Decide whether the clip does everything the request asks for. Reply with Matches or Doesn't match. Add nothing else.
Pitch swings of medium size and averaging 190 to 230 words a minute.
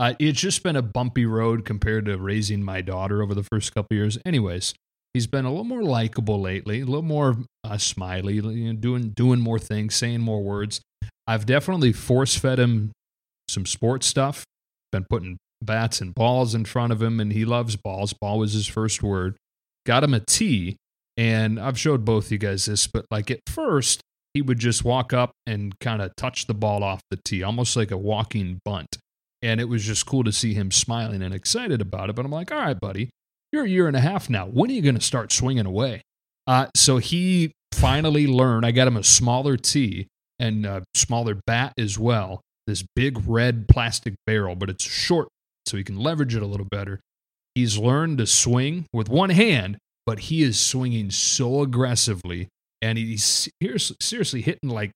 Matches